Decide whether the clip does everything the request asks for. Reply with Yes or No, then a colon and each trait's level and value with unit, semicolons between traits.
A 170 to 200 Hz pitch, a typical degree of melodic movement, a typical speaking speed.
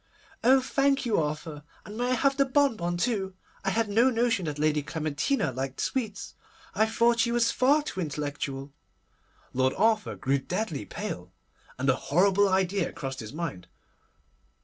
No: high, 190 Hz; wide, 8.1 semitones; average, 160 wpm